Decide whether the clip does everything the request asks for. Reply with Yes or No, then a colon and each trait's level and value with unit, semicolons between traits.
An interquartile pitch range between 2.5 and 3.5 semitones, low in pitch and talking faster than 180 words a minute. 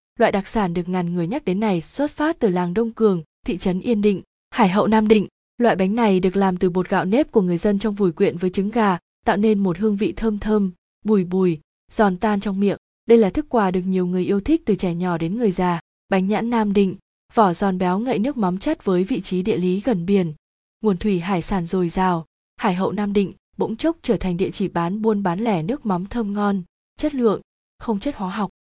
No: average, 3.2 semitones; high, 200 Hz; average, 245 wpm